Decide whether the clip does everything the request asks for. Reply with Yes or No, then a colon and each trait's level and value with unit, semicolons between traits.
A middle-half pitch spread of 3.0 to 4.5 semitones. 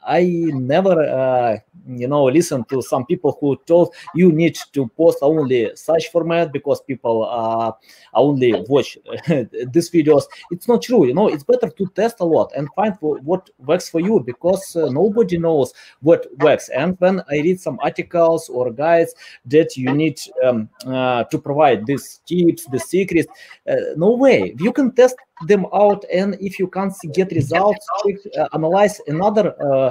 No: average, 5.2 semitones